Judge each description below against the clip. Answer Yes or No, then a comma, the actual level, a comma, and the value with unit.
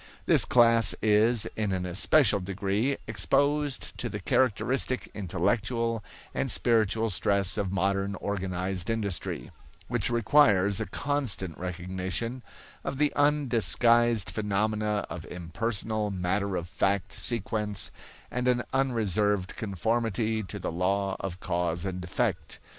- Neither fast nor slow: No, slow, 120 wpm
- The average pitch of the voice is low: Yes, low, 105 Hz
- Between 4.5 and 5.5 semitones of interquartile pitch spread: No, average, 3.7 semitones